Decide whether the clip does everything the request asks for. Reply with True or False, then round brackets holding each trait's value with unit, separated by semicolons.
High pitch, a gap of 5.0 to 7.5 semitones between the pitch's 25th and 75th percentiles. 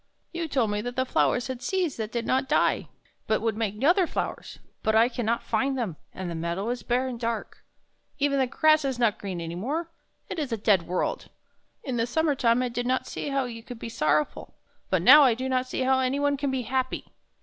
False (245 Hz; 3.4 semitones)